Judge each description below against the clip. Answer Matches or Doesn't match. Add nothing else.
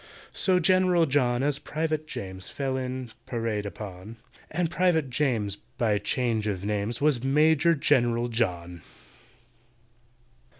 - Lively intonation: Matches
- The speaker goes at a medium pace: Doesn't match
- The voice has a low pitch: Matches